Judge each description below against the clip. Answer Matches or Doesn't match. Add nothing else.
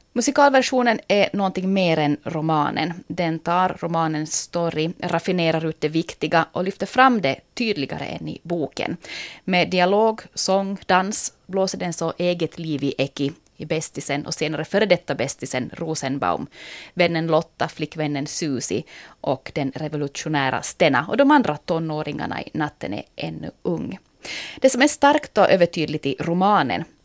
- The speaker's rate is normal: Matches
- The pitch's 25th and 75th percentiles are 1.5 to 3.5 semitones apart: Doesn't match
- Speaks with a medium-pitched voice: Matches